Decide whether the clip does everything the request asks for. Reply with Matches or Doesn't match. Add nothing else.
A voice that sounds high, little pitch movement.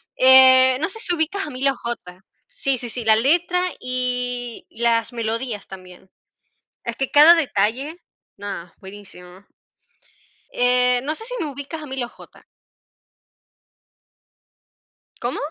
Doesn't match